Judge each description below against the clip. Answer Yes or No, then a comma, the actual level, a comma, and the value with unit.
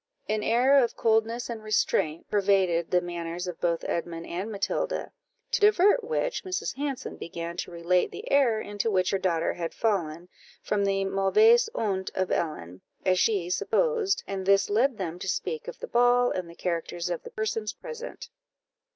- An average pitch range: No, wide, 5.8 semitones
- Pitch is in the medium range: No, high, 200 Hz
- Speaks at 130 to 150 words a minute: No, average, 175 wpm